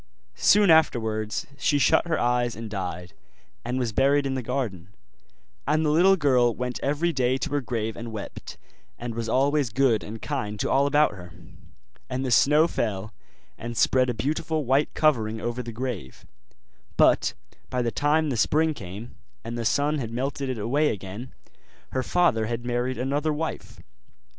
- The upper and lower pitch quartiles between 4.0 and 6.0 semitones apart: Yes, average, 4.3 semitones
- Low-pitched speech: Yes, low, 125 Hz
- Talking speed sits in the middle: Yes, average, 170 wpm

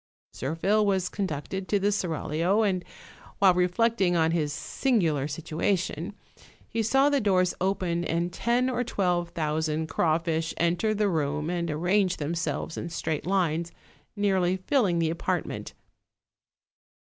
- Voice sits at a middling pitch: Yes, medium, 175 Hz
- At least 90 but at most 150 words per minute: Yes, slow, 135 wpm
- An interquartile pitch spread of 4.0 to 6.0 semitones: No, average, 3.6 semitones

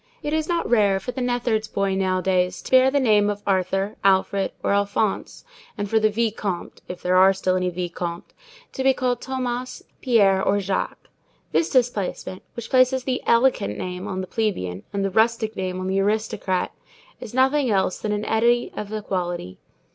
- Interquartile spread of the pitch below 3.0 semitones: No, average, 4.3 semitones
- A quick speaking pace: No, average, 175 wpm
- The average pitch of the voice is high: Yes, high, 205 Hz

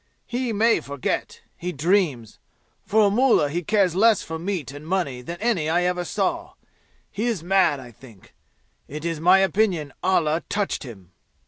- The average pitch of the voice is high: No, medium, 175 Hz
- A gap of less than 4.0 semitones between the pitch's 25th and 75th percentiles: No, wide, 5.5 semitones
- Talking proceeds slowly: No, average, 165 wpm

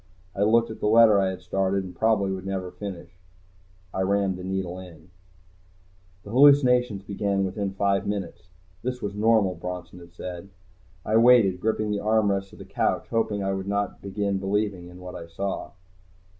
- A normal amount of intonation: No, narrow, 2.2 semitones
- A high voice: No, low, 100 Hz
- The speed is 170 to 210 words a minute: Yes, average, 175 wpm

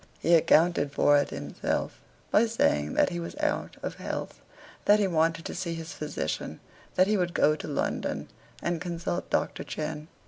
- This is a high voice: No, medium, 170 Hz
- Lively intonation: No, average, 2.9 semitones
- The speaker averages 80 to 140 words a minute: No, average, 175 wpm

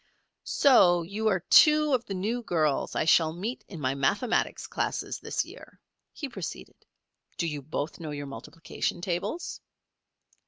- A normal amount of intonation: No, wide, 6.5 semitones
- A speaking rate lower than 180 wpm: Yes, average, 150 wpm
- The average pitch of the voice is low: No, medium, 175 Hz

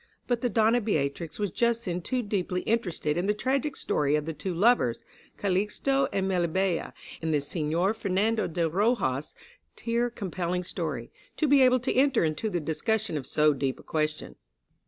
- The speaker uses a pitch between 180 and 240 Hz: Yes, high, 190 Hz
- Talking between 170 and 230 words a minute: Yes, average, 175 wpm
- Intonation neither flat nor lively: No, wide, 6.3 semitones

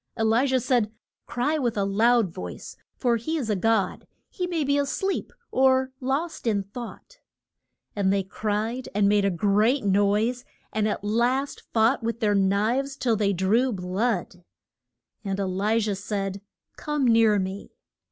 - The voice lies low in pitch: No, high, 220 Hz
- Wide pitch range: No, average, 4.3 semitones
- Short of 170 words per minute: No, average, 180 wpm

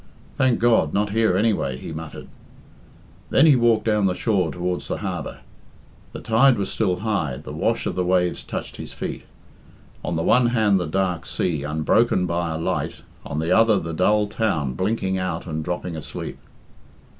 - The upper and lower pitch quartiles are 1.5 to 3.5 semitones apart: No, average, 4.9 semitones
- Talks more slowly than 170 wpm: No, average, 180 wpm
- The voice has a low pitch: Yes, very low, 95 Hz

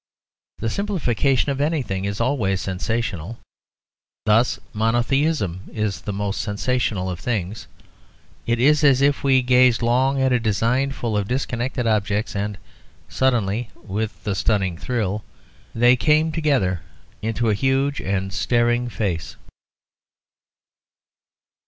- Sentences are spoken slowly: Yes, slow, 120 wpm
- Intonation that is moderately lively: Yes, average, 4.5 semitones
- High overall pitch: No, low, 115 Hz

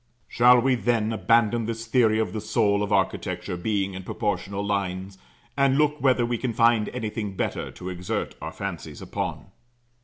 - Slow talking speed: No, average, 165 wpm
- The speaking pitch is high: No, low, 110 Hz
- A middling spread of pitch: Yes, average, 3.0 semitones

